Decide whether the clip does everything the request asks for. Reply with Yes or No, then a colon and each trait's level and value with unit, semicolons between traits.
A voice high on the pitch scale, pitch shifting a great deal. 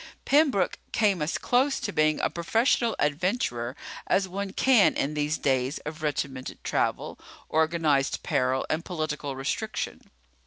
No: medium, 155 Hz; wide, 5.9 semitones